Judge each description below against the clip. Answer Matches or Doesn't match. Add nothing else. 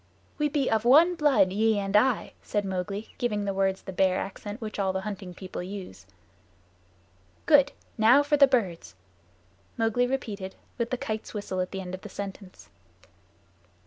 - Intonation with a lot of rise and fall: Doesn't match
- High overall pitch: Matches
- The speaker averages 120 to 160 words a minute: Doesn't match